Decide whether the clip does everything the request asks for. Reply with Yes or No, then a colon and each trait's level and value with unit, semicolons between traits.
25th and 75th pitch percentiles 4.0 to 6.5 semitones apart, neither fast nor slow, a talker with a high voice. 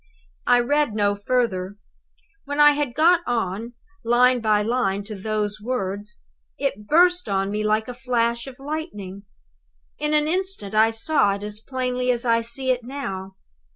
Yes: average, 4.3 semitones; average, 160 wpm; high, 235 Hz